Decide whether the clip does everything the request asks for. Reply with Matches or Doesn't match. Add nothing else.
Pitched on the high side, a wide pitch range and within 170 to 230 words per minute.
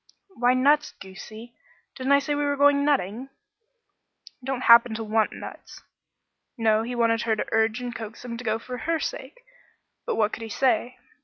Doesn't match